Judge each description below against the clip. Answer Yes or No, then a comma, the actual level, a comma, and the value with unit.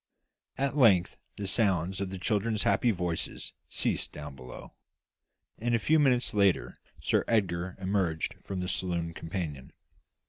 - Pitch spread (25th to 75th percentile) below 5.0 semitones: Yes, average, 4.0 semitones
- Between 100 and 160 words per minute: Yes, average, 140 wpm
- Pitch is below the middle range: Yes, very low, 95 Hz